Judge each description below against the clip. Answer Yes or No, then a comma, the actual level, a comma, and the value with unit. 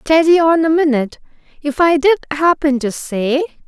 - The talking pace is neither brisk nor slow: Yes, average, 165 wpm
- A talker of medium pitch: No, very high, 300 Hz